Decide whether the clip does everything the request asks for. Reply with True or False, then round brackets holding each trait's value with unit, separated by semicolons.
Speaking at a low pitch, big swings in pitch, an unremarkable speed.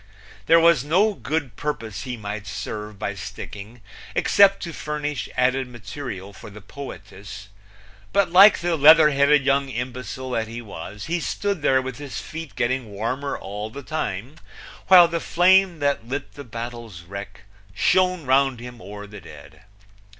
True (130 Hz; 6.3 semitones; 160 wpm)